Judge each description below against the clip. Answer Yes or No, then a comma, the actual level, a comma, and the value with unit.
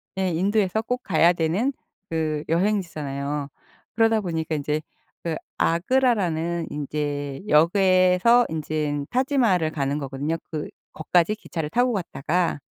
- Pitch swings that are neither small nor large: Yes, average, 4.8 semitones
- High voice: No, medium, 165 Hz